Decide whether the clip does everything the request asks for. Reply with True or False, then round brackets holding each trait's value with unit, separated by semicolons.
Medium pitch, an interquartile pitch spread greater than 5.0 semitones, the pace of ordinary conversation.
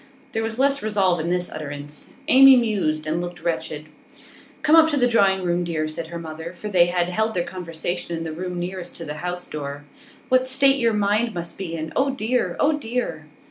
False (180 Hz; 5.6 semitones; 215 wpm)